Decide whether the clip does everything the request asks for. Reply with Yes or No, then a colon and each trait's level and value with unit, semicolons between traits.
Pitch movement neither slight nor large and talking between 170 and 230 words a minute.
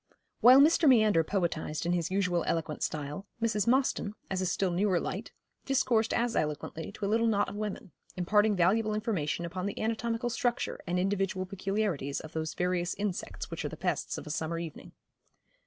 Yes: average, 4.2 semitones; average, 180 wpm